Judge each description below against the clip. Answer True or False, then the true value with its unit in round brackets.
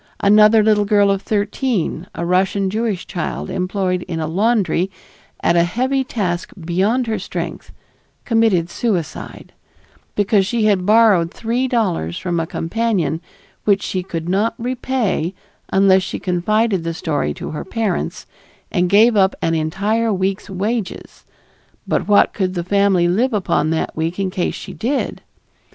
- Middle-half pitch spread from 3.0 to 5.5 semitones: True (4.0 semitones)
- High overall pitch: True (195 Hz)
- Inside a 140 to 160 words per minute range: True (150 wpm)